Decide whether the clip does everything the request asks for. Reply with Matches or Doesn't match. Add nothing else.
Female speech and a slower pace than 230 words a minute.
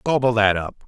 Doesn't match